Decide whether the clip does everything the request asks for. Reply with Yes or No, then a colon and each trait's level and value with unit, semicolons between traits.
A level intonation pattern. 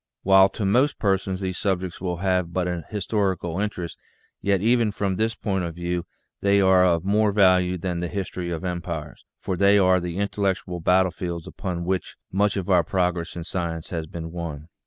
Yes: narrow, 2.2 semitones